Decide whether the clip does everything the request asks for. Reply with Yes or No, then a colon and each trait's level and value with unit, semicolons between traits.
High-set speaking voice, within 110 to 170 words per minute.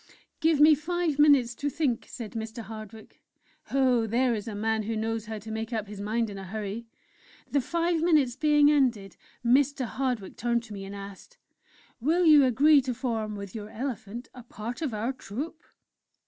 No: high, 235 Hz; average, 185 wpm